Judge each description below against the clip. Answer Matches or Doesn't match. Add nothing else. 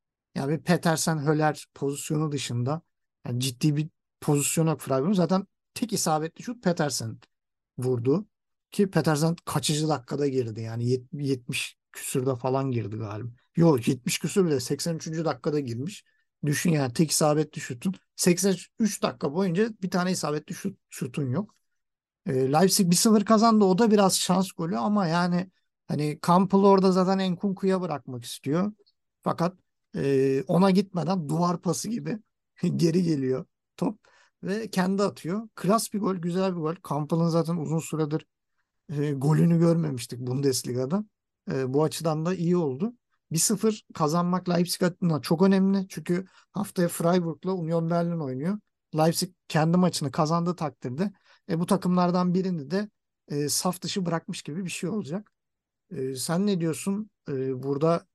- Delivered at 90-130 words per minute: Doesn't match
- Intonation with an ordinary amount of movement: Matches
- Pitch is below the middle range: Doesn't match